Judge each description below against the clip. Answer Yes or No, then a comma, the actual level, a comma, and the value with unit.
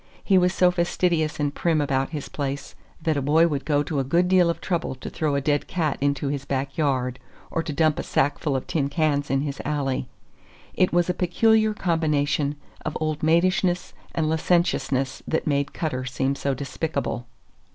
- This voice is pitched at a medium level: Yes, medium, 150 Hz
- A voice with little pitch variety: No, average, 3.3 semitones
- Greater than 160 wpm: Yes, average, 190 wpm